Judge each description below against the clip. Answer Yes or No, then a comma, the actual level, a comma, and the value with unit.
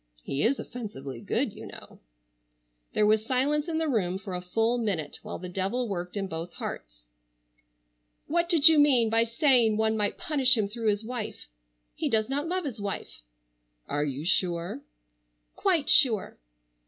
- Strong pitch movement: Yes, wide, 6.4 semitones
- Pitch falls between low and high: No, high, 220 Hz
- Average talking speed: Yes, average, 165 wpm